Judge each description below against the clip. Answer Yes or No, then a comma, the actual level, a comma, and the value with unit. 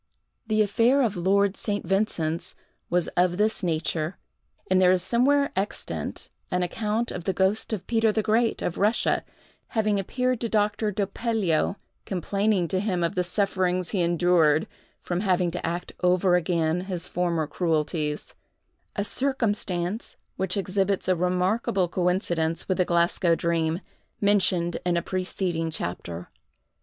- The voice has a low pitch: No, medium, 185 Hz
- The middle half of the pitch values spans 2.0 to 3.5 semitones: Yes, average, 3.2 semitones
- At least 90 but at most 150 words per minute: Yes, average, 145 wpm